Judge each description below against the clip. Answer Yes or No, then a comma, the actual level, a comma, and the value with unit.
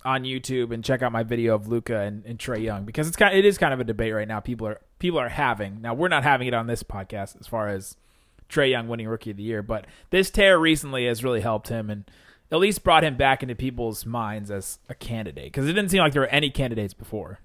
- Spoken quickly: Yes, fast, 270 wpm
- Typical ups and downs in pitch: Yes, average, 3.8 semitones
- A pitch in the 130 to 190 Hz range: No, low, 115 Hz